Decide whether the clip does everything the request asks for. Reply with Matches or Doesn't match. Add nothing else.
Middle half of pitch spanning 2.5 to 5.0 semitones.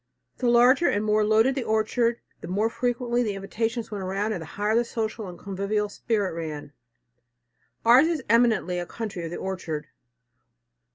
Matches